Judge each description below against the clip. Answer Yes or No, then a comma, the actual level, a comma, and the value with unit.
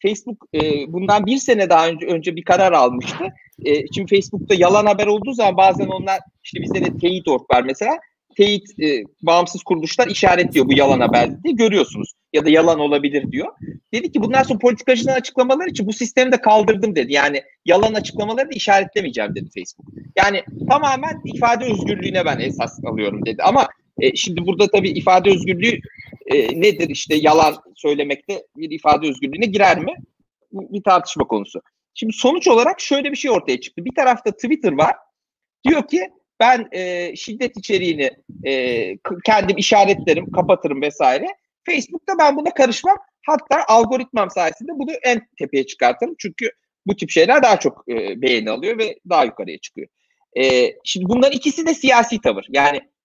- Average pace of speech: No, fast, 160 wpm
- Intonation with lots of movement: Yes, wide, 6.8 semitones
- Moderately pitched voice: No, high, 210 Hz